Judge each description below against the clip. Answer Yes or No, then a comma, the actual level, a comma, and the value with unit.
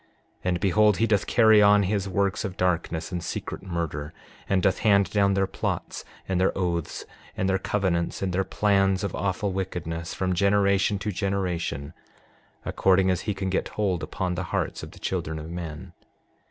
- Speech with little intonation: Yes, narrow, 2.1 semitones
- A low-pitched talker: Yes, very low, 95 Hz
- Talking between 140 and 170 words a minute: No, average, 180 wpm